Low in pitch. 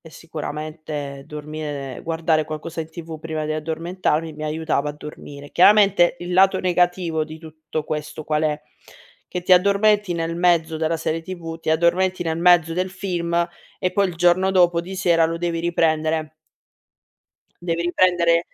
No: medium, 165 Hz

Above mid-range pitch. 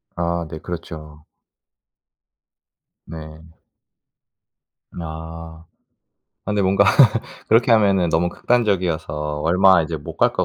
No: very low, 85 Hz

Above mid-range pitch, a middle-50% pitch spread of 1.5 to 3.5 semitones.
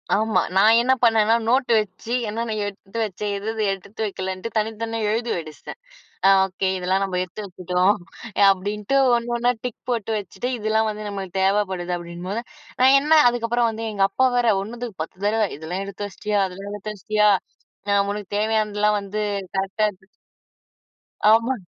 Yes: high, 210 Hz; average, 2.8 semitones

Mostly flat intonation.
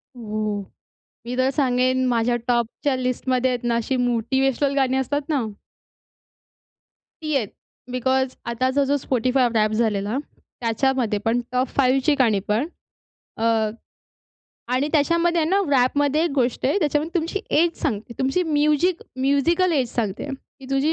No: average, 3.3 semitones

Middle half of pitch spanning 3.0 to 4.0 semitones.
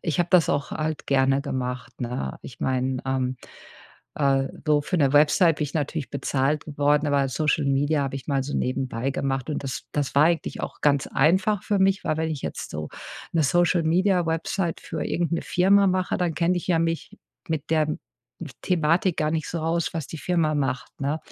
Yes: average, 3.5 semitones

